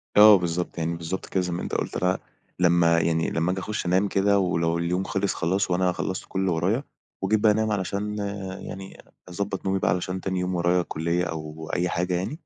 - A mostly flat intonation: Yes, narrow, 2.2 semitones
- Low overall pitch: Yes, very low, 90 Hz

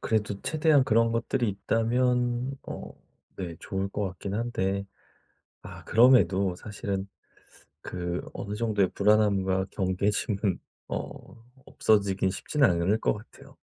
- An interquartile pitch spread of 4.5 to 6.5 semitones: No, average, 3.4 semitones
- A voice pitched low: Yes, low, 105 Hz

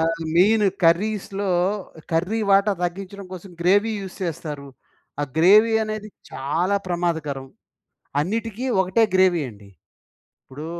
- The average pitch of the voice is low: No, medium, 185 Hz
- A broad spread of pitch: No, average, 3.7 semitones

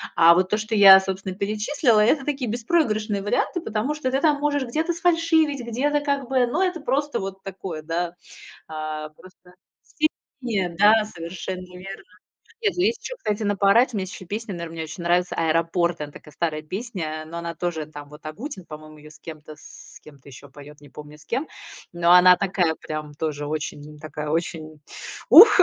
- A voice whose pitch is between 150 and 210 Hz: Yes, medium, 185 Hz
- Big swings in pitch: Yes, wide, 7.3 semitones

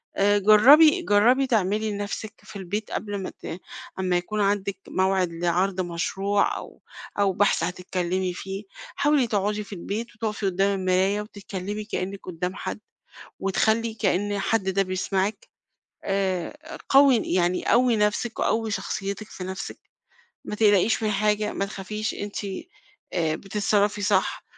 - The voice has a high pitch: Yes, high, 200 Hz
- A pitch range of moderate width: No, narrow, 2.2 semitones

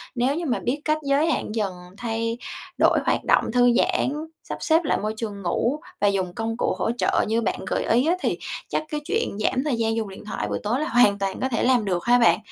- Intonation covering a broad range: No, average, 4.3 semitones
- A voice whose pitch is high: Yes, high, 235 Hz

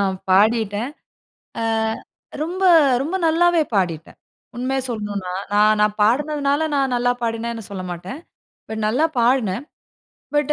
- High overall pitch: Yes, high, 235 Hz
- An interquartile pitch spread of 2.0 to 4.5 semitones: No, wide, 5.5 semitones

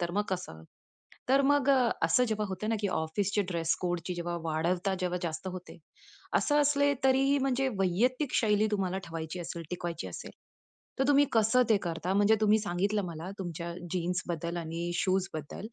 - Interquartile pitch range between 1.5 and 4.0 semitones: No, average, 4.4 semitones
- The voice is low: No, medium, 185 Hz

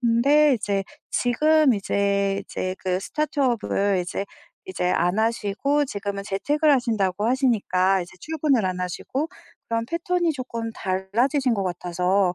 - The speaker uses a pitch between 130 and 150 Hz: No, high, 220 Hz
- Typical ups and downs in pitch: No, wide, 6.2 semitones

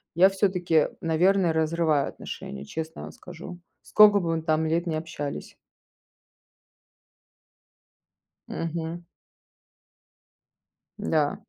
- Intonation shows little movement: Yes, narrow, 1.9 semitones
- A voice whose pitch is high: No, medium, 165 Hz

